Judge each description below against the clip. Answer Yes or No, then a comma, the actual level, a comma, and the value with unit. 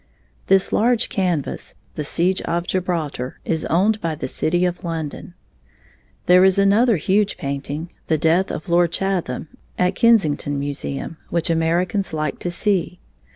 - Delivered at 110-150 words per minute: Yes, average, 145 wpm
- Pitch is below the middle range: No, medium, 175 Hz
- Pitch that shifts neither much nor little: Yes, average, 3.4 semitones